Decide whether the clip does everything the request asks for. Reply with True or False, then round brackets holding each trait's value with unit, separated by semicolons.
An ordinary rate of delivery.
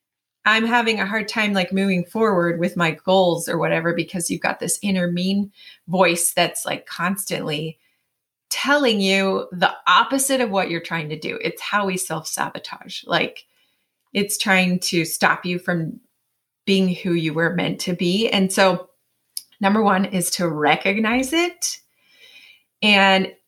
True (155 wpm)